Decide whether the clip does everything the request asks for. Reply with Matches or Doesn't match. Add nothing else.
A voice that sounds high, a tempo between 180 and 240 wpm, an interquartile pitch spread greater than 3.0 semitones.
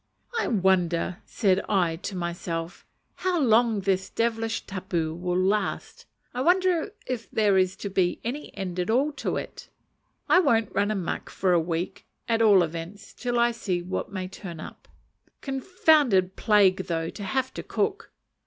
Doesn't match